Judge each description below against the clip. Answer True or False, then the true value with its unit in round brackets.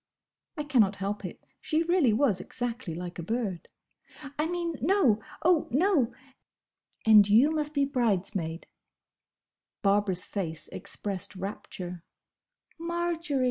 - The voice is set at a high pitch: True (230 Hz)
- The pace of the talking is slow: True (115 wpm)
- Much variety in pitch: True (7.9 semitones)